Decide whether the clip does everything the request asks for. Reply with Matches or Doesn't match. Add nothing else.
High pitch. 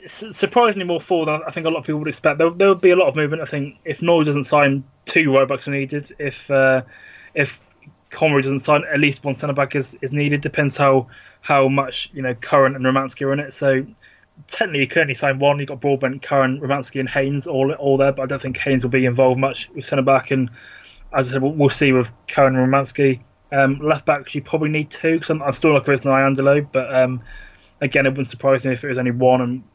Doesn't match